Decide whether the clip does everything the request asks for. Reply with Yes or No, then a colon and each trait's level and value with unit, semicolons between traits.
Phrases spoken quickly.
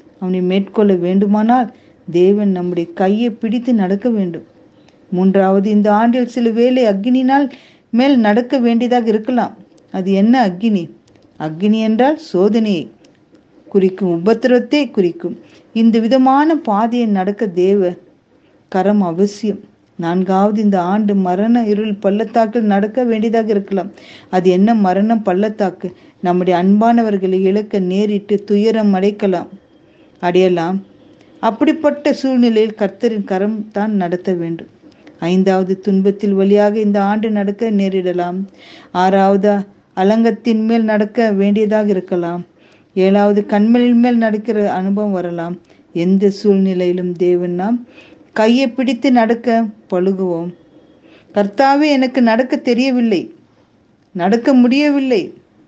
No: average, 100 wpm